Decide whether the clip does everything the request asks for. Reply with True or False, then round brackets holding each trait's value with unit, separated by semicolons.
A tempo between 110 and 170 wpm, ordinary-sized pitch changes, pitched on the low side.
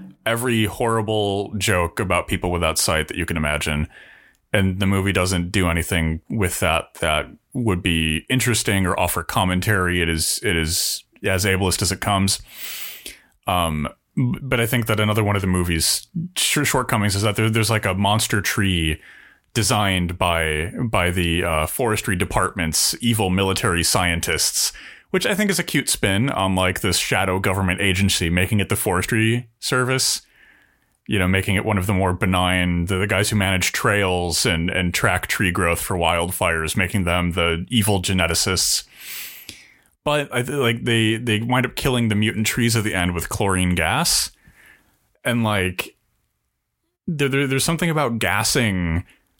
True (165 wpm; 4.4 semitones; 100 Hz)